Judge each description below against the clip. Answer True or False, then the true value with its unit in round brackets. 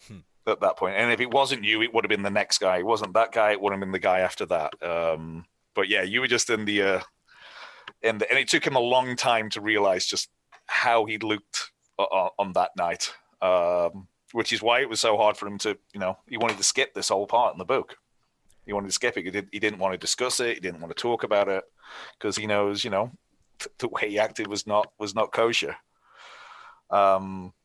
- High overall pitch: False (105 Hz)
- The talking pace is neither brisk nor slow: False (245 wpm)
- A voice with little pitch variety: False (3.0 semitones)